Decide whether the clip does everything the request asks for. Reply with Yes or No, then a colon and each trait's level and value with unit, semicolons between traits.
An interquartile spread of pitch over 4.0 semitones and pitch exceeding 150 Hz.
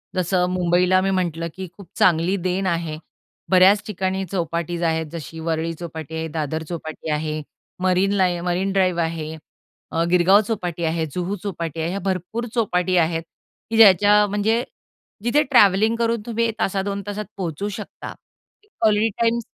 No: average, 3.4 semitones; medium, 185 Hz